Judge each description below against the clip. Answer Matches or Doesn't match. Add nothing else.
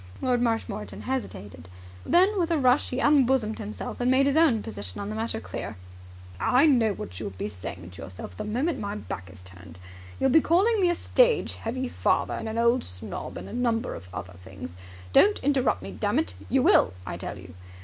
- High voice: Matches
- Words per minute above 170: Matches